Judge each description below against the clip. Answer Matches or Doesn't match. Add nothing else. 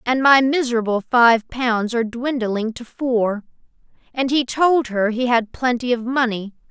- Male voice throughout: Doesn't match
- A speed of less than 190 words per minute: Matches